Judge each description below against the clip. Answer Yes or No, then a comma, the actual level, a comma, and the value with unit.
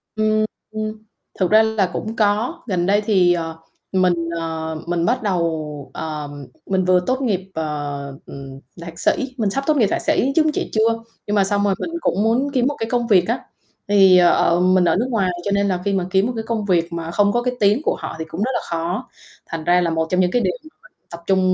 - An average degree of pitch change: Yes, average, 4.6 semitones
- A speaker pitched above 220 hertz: No, high, 195 Hz